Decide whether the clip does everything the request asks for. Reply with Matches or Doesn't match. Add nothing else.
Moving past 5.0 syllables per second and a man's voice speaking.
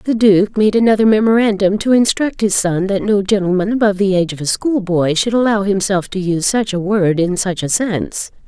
Doesn't match